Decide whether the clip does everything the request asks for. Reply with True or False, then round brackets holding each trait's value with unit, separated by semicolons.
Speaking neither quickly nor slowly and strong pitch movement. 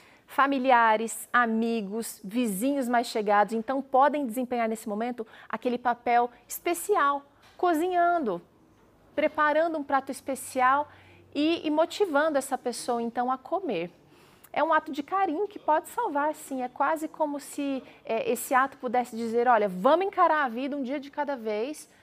False (145 wpm; 4.1 semitones)